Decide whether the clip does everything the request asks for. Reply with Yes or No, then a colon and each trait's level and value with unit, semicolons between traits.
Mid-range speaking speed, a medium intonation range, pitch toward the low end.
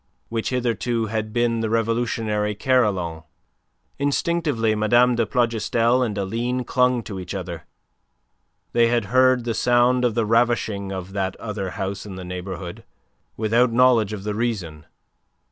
Yes: average, 145 wpm; average, 3.4 semitones; low, 115 Hz